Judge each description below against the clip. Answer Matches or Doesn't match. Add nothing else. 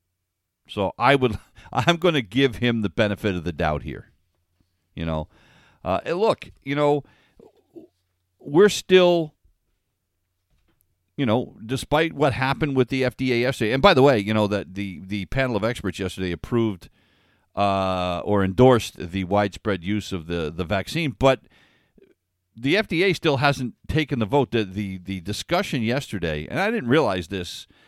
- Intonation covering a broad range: Matches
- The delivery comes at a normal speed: Matches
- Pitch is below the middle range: Matches